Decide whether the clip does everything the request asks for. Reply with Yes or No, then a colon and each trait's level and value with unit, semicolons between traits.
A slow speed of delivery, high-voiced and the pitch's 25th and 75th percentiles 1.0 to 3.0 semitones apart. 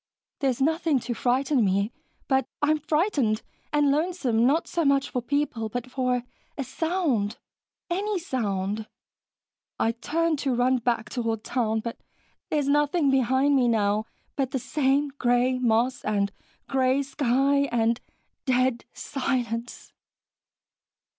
No: slow, 130 wpm; very high, 260 Hz; average, 3.5 semitones